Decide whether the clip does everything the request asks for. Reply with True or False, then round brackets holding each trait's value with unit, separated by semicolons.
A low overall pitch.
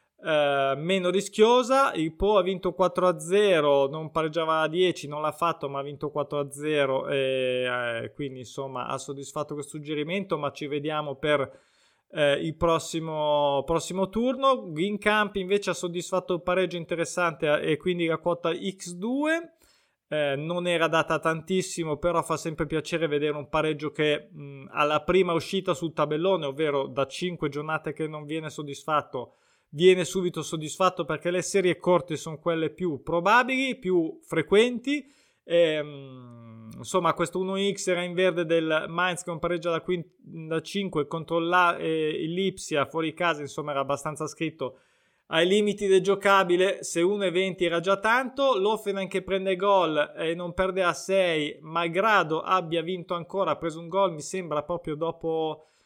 False (165 Hz)